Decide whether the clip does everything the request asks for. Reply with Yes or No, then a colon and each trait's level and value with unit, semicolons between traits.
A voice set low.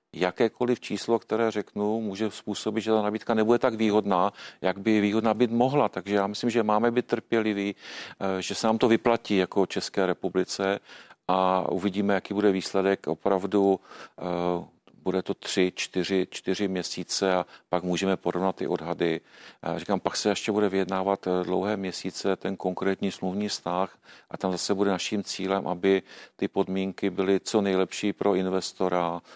Yes: very low, 95 Hz